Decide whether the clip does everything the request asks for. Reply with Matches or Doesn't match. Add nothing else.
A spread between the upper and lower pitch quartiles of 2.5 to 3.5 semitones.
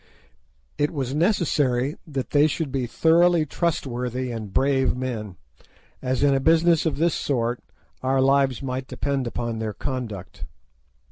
Matches